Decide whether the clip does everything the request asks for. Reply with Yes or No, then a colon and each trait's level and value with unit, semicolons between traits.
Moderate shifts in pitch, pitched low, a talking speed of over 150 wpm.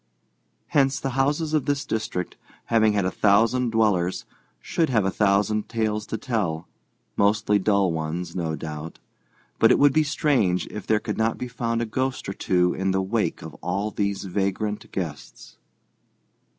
Yes: average, 3.9 semitones; low, 105 Hz; average, 165 wpm